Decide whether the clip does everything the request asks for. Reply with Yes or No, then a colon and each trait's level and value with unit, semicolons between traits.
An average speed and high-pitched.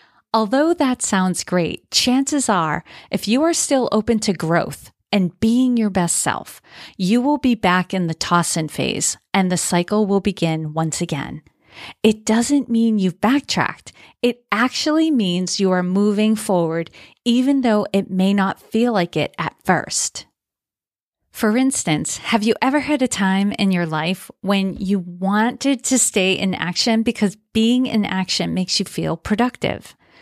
Yes: average, 165 wpm; high, 210 Hz